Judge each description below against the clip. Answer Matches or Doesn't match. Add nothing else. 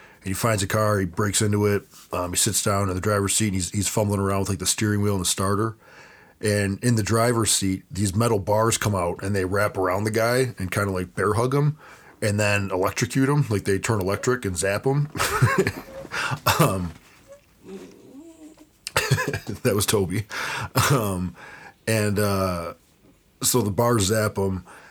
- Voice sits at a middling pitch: Doesn't match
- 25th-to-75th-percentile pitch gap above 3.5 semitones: Doesn't match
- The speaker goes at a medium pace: Matches